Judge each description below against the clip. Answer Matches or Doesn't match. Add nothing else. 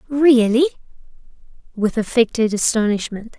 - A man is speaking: Doesn't match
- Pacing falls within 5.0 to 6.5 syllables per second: Doesn't match